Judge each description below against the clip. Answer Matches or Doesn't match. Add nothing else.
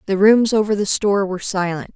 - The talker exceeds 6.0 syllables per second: Matches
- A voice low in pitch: Doesn't match